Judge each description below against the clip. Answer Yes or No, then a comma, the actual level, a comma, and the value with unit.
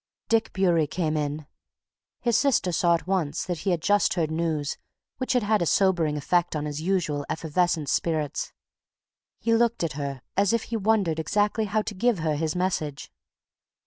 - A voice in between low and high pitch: Yes, medium, 175 Hz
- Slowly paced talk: No, average, 180 wpm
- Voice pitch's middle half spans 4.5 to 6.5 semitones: Yes, average, 4.9 semitones